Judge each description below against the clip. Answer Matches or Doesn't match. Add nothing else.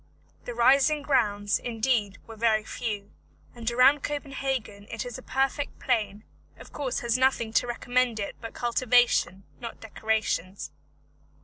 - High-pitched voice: Matches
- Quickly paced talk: Doesn't match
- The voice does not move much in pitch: Doesn't match